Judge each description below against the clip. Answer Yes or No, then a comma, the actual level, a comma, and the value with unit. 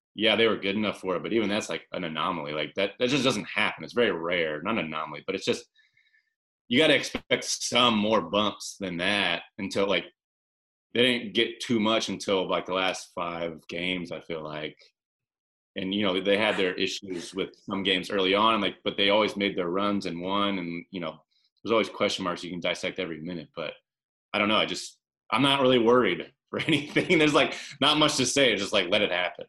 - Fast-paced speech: Yes, fast, 225 wpm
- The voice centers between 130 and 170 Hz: No, low, 100 Hz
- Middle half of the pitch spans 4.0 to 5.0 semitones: Yes, average, 4.7 semitones